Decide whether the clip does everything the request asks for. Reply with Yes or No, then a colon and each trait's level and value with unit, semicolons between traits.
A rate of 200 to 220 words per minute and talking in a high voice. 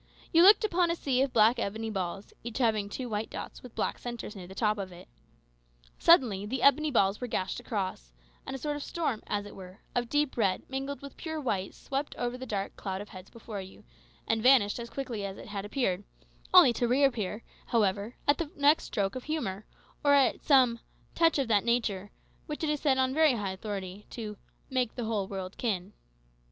Yes: fast, 205 wpm; high, 230 Hz